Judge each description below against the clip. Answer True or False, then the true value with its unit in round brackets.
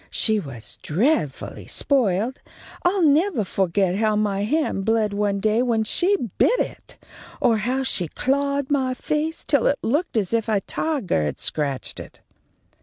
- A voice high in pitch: True (225 Hz)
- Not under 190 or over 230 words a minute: False (155 wpm)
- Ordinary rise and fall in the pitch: False (6.1 semitones)